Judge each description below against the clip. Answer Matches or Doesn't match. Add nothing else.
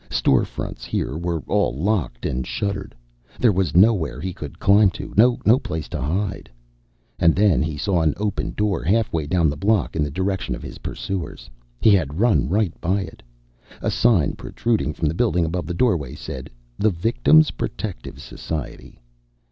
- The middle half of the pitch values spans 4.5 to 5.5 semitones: Matches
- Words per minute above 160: Matches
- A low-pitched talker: Matches